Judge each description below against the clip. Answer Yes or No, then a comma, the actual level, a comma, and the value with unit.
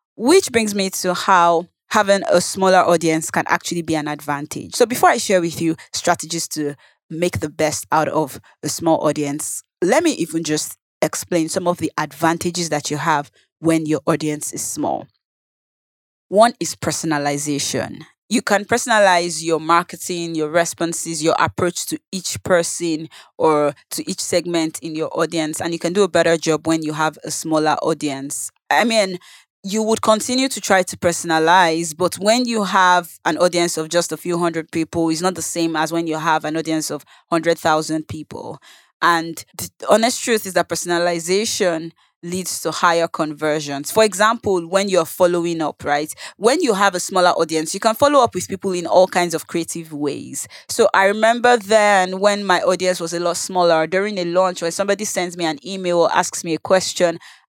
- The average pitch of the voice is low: No, medium, 170 Hz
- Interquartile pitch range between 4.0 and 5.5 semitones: No, average, 3.0 semitones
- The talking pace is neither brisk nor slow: Yes, average, 185 wpm